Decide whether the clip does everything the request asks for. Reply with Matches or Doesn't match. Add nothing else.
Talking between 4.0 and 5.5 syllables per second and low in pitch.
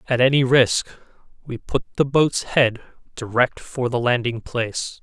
Matches